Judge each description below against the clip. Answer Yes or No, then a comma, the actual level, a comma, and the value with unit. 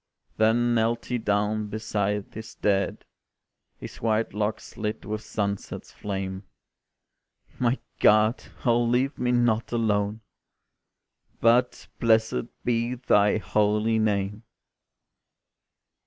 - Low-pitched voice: Yes, low, 110 Hz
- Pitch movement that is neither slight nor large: No, narrow, 2.1 semitones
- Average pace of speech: No, slow, 100 wpm